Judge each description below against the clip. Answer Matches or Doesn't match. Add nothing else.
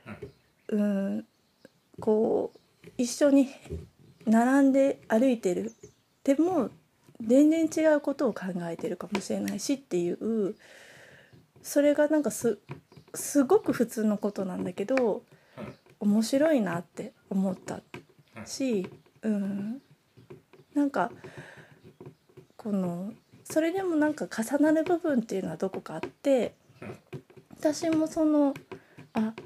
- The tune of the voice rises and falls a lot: Matches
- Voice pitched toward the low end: Doesn't match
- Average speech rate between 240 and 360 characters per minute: Doesn't match